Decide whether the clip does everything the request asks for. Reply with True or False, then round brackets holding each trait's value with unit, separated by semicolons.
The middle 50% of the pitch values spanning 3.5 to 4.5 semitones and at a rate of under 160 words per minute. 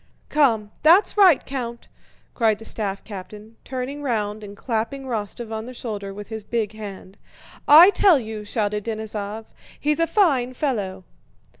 True (4.1 semitones; 150 wpm)